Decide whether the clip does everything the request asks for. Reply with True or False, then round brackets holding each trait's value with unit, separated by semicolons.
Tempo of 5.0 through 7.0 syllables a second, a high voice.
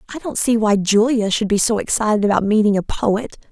True (5.8 syllables/s; 215 Hz)